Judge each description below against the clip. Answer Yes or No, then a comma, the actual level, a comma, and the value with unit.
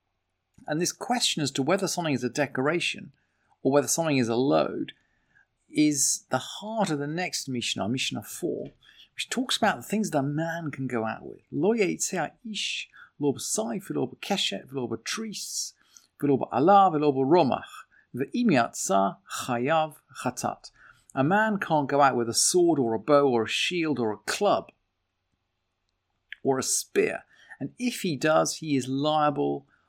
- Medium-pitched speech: Yes, medium, 145 Hz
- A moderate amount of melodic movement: No, wide, 6.3 semitones